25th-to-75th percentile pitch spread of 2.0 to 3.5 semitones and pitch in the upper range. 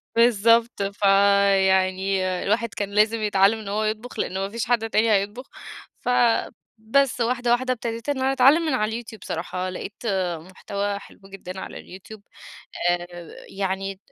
Yes: average, 3.1 semitones; high, 215 Hz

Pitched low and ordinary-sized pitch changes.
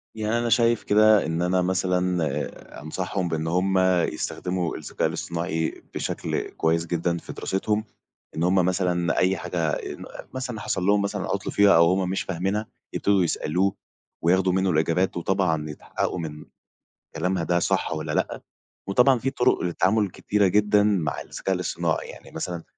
Yes: very low, 90 Hz; average, 3.2 semitones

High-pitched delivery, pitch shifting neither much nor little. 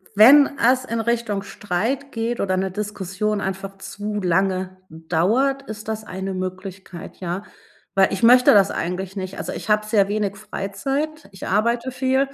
Yes: high, 205 Hz; average, 3.7 semitones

